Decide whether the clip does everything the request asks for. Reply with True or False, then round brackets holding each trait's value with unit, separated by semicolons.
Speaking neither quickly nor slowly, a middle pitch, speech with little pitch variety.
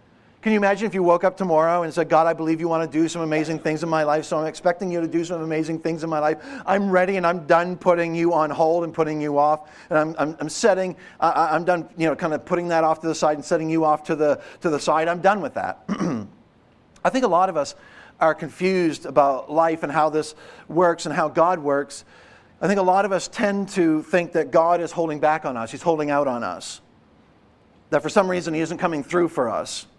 False (255 wpm; 165 Hz; 2.2 semitones)